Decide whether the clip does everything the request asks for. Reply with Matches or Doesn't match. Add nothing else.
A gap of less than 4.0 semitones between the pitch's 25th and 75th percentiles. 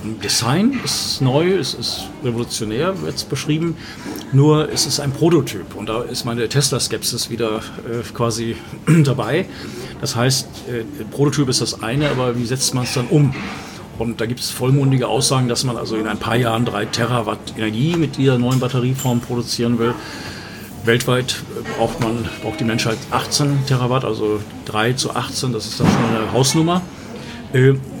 Matches